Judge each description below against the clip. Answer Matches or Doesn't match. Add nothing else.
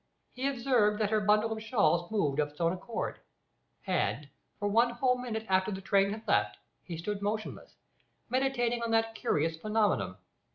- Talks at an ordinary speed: Matches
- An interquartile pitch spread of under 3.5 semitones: Doesn't match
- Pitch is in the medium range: Doesn't match